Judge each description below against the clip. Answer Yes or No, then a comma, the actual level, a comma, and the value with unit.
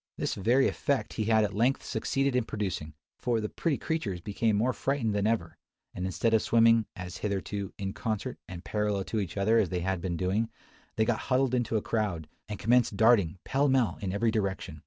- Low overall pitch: Yes, low, 110 Hz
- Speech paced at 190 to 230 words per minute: Yes, average, 200 wpm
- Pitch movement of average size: Yes, average, 3.3 semitones